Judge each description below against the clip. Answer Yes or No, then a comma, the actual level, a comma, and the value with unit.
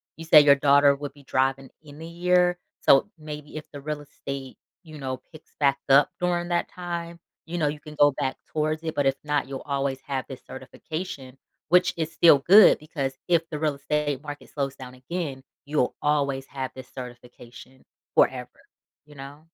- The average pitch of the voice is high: No, medium, 145 Hz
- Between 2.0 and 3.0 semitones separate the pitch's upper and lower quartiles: Yes, average, 2.7 semitones